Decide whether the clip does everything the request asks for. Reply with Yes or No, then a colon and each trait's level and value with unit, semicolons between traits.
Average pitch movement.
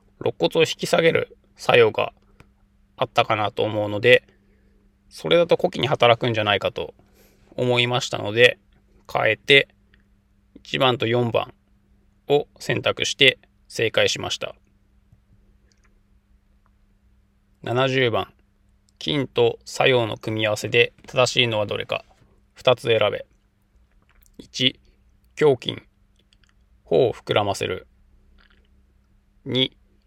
Yes: average, 4.2 semitones